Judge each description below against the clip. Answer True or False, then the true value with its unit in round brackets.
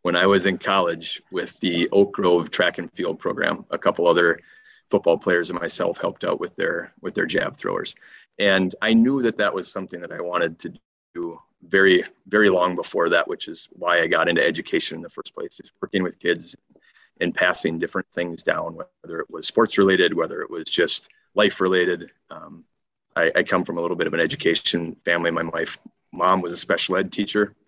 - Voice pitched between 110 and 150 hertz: False (90 Hz)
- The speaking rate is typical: False (210 wpm)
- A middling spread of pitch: True (3.2 semitones)